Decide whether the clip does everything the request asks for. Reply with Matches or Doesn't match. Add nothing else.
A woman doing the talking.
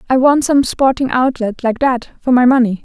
Matches